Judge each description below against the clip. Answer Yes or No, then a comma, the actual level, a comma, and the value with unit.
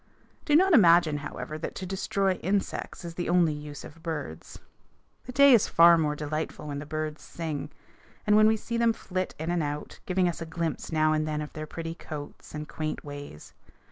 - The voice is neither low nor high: Yes, medium, 165 Hz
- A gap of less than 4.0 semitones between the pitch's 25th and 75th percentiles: Yes, average, 3.5 semitones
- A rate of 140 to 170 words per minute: No, fast, 205 wpm